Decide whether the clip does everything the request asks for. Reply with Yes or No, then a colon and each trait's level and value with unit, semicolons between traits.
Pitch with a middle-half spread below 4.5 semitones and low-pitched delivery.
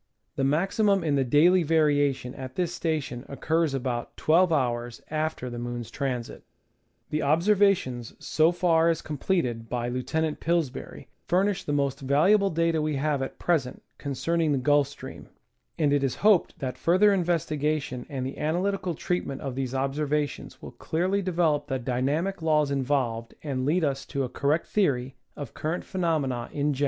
No: average, 4.1 semitones; medium, 150 Hz